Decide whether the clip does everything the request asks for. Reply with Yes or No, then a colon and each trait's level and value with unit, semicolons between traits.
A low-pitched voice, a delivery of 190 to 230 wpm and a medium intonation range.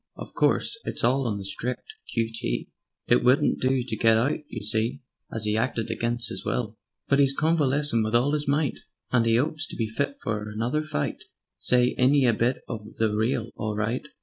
Yes: low, 120 Hz; fast, 205 wpm; average, 3.6 semitones